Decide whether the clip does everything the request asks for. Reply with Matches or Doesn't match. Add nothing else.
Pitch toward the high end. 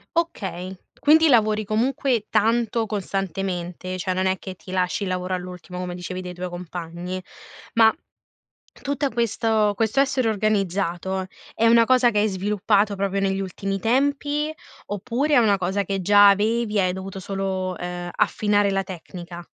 Matches